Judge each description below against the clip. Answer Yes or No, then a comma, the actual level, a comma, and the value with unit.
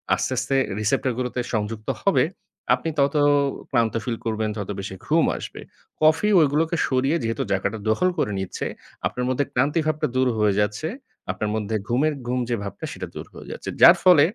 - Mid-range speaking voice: No, low, 125 Hz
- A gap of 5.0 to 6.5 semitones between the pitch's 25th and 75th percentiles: Yes, average, 5.3 semitones